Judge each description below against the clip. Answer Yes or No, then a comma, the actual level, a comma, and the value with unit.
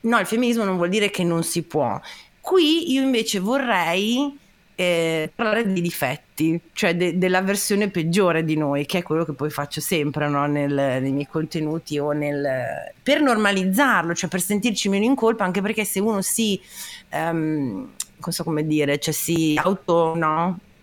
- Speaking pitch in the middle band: Yes, medium, 180 Hz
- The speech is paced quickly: Yes, fast, 175 wpm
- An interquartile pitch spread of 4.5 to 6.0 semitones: Yes, average, 5.2 semitones